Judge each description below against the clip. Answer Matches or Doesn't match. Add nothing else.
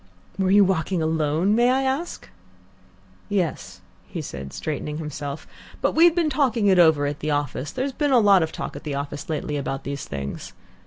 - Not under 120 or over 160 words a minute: Doesn't match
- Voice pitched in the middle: Matches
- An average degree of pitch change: Doesn't match